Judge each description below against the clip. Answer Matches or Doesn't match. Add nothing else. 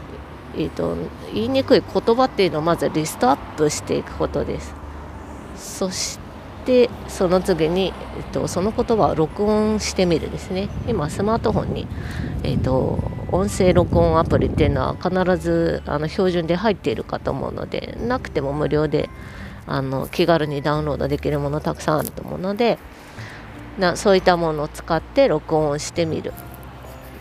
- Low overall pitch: Doesn't match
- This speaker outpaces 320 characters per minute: Matches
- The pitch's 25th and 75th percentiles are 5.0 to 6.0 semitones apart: Doesn't match